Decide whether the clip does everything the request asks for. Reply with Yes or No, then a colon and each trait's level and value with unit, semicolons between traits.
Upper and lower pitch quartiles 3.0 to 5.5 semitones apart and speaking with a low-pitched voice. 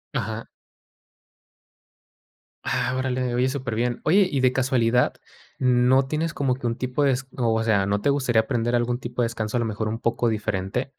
No: narrow, 2.4 semitones; low, 125 Hz